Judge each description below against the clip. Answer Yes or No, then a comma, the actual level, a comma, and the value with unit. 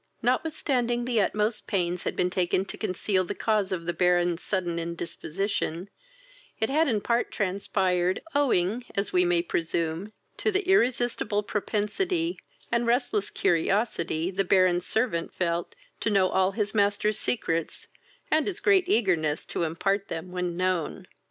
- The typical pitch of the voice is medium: No, high, 195 Hz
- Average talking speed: Yes, average, 145 wpm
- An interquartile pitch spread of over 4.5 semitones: Yes, average, 4.9 semitones